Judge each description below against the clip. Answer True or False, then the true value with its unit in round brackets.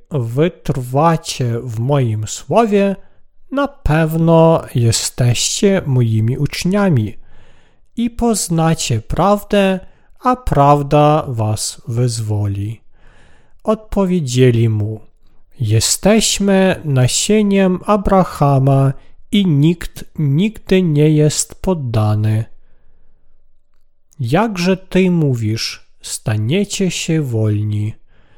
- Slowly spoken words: True (70 wpm)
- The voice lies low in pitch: False (145 Hz)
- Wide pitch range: True (8.6 semitones)